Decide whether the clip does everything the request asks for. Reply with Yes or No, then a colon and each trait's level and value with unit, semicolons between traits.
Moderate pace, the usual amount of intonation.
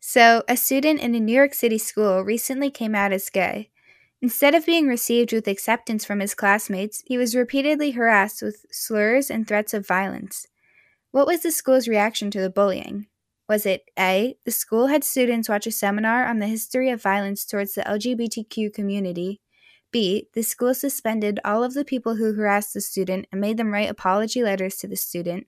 Yes: average, 190 wpm; average, 3.6 semitones